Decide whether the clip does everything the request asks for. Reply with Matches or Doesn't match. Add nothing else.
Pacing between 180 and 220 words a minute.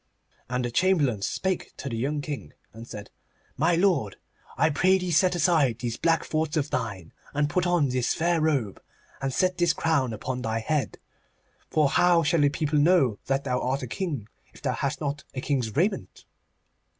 Matches